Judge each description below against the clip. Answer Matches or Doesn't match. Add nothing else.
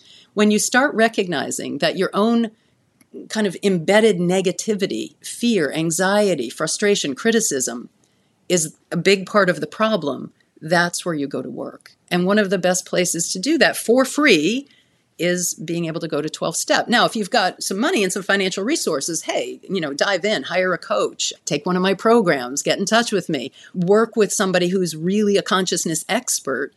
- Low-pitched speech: Doesn't match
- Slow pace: Doesn't match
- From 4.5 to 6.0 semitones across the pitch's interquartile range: Doesn't match